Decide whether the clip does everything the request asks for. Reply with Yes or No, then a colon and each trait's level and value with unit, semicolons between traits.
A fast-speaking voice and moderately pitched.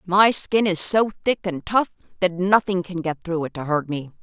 Yes: fast, 225 wpm; medium, 180 Hz